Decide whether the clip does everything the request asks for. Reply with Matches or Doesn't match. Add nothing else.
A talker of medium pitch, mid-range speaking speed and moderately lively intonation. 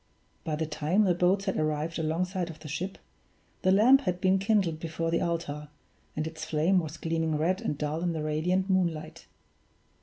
Matches